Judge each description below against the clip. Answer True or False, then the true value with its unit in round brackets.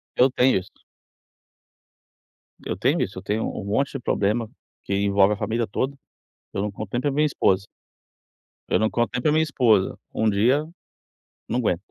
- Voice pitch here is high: False (110 Hz)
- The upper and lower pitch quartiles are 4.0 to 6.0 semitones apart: True (4.3 semitones)